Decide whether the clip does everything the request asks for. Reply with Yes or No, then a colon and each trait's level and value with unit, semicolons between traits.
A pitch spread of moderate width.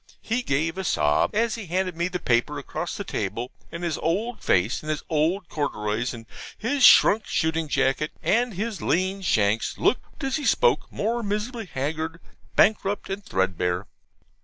No: wide, 7.8 semitones